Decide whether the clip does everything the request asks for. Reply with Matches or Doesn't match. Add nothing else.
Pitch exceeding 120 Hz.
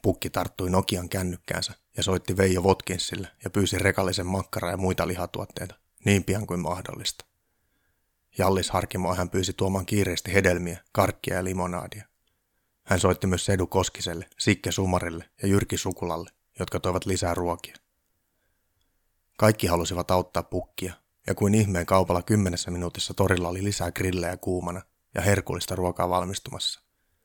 Doesn't match